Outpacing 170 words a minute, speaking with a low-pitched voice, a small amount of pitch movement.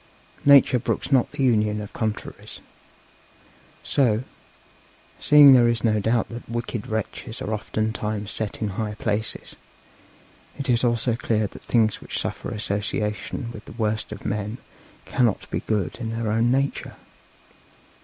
No: average, 145 wpm; low, 110 Hz; narrow, 2.1 semitones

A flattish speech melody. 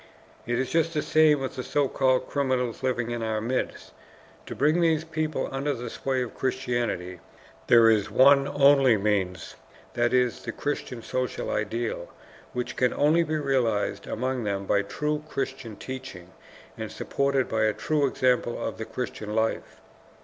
No: average, 3.7 semitones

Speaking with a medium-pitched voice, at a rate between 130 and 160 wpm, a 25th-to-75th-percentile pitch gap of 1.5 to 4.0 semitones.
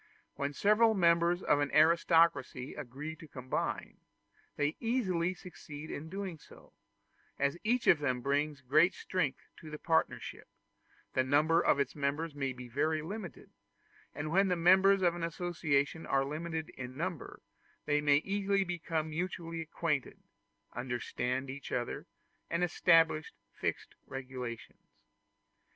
Yes: medium, 155 Hz; slow, 135 wpm; average, 3.7 semitones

